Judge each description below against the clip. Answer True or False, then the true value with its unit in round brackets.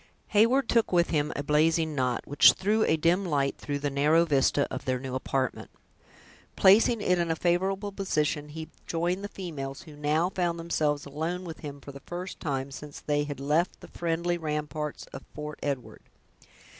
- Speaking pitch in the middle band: True (155 Hz)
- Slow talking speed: False (180 wpm)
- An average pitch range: True (3.3 semitones)